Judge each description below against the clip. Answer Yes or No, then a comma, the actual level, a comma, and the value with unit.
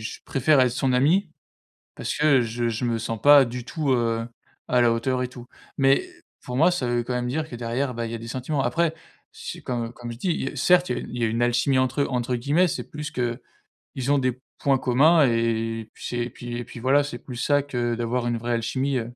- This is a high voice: No, low, 125 Hz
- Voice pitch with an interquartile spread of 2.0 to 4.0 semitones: Yes, average, 2.9 semitones